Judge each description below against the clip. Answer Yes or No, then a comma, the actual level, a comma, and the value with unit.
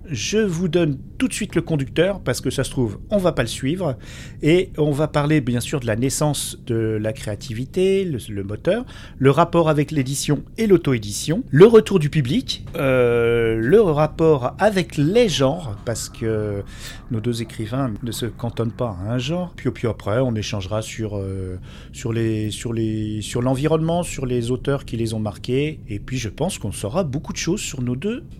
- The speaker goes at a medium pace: Yes, average, 205 wpm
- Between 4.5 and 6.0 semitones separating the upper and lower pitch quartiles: Yes, wide, 5.4 semitones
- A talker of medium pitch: No, low, 130 Hz